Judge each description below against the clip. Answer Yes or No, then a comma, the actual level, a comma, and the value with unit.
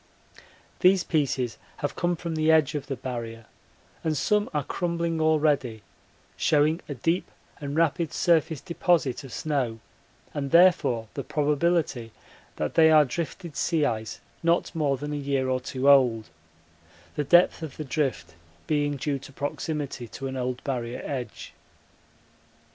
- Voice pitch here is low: No, medium, 145 Hz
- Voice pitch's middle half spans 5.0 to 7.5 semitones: No, average, 3.7 semitones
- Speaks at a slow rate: No, average, 150 wpm